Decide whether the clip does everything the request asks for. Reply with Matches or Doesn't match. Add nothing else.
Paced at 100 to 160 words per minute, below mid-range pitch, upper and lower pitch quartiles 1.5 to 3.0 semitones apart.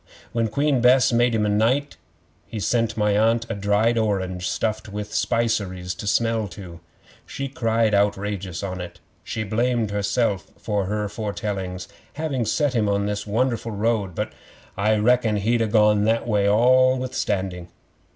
Matches